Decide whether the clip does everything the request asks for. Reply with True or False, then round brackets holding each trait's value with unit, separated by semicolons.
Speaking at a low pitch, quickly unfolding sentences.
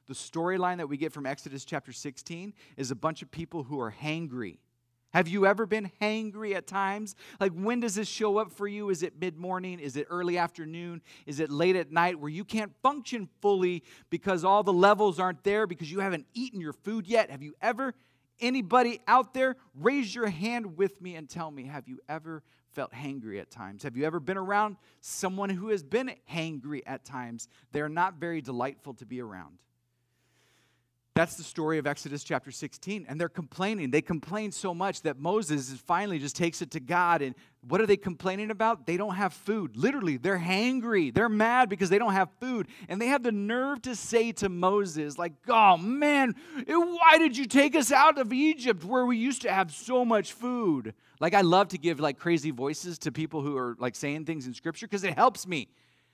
False (180 Hz; 210 wpm)